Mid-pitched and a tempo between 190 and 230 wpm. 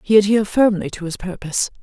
No: high, 195 Hz; average, 200 wpm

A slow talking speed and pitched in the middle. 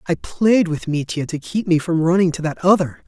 No: fast, 235 wpm; medium, 170 Hz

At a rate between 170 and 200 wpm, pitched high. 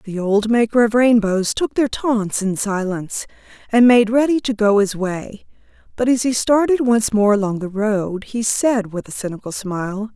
Yes: average, 190 wpm; high, 220 Hz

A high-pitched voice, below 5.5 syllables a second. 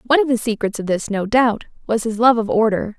No: high, 225 Hz; 6.0 syllables/s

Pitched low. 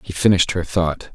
Yes: very low, 90 Hz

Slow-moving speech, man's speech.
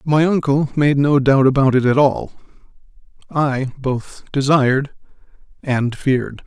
Yes: slow, 130 wpm; male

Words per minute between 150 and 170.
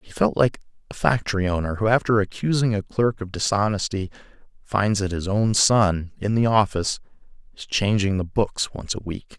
No: average, 180 wpm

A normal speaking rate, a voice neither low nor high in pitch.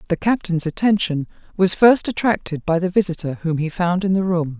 Yes: average, 195 wpm; medium, 180 Hz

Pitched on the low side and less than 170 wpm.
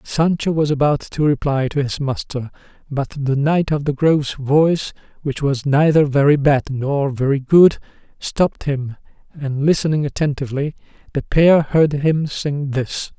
No: medium, 145 Hz; average, 155 wpm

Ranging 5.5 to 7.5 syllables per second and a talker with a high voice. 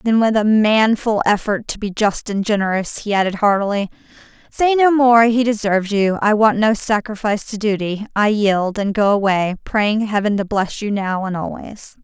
No: 4.9 syllables/s; high, 210 Hz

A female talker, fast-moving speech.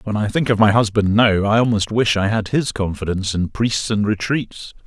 No: male; fast, 220 wpm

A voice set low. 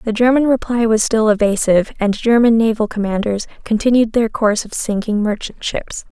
No: high, 220 Hz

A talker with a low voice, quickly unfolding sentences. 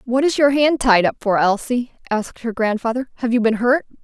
No: high, 240 Hz; fast, 225 wpm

